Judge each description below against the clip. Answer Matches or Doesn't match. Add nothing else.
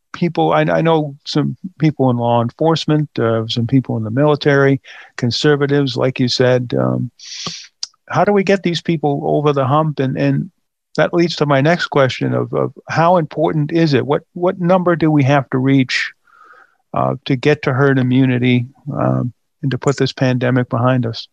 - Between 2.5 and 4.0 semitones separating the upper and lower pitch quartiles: Matches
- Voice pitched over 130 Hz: Matches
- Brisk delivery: Doesn't match